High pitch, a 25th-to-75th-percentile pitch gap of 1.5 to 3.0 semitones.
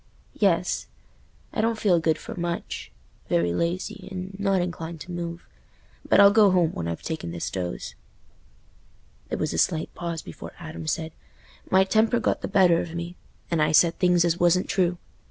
No: medium, 170 Hz; narrow, 2.6 semitones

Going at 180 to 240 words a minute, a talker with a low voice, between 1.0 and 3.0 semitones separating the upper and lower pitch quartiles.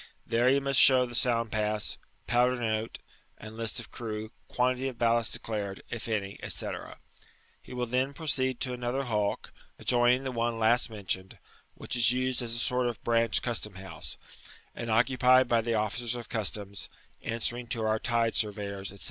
No: average, 170 wpm; low, 115 Hz; narrow, 2.4 semitones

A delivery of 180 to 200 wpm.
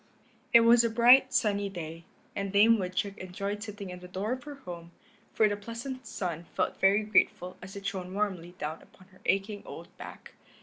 Yes: average, 190 wpm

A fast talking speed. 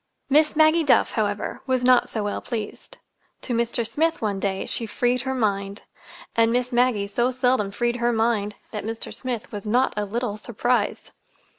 No: average, 170 wpm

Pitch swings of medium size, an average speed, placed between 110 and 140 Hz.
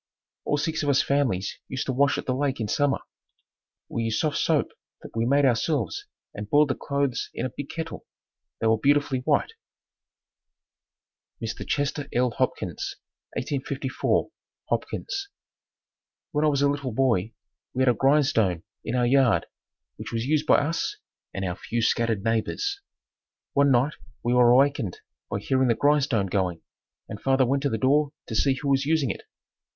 Yes: average, 3.8 semitones; average, 170 wpm; low, 135 Hz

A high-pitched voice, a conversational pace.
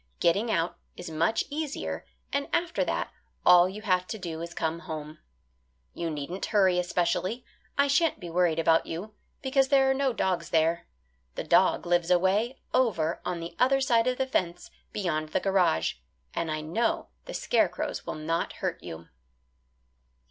No: medium, 180 Hz; average, 170 wpm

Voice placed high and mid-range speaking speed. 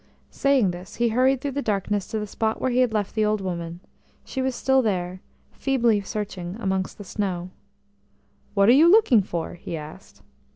Yes: high, 210 Hz; average, 190 wpm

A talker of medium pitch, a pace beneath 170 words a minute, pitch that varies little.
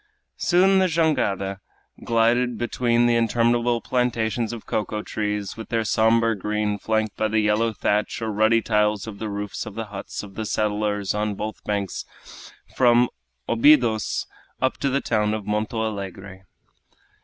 No: low, 110 Hz; average, 150 wpm; narrow, 2.1 semitones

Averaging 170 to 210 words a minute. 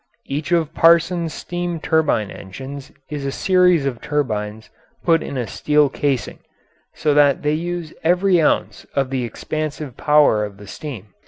No: average, 155 wpm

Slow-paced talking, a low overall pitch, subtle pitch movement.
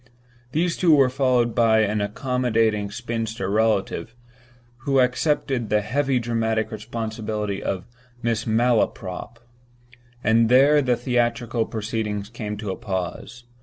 Yes: slow, 115 wpm; low, 115 Hz; narrow, 2.3 semitones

